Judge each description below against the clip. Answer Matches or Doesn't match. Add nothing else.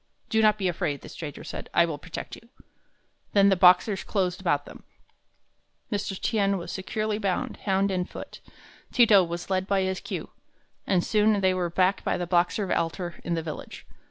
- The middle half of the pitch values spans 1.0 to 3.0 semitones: Matches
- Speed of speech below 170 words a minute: Doesn't match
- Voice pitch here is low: Doesn't match